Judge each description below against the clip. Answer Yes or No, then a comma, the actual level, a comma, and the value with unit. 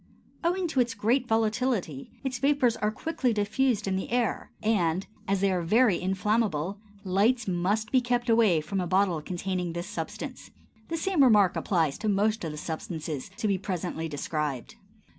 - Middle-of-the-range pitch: No, high, 205 Hz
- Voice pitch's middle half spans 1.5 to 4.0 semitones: No, average, 5.3 semitones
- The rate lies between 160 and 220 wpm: Yes, average, 170 wpm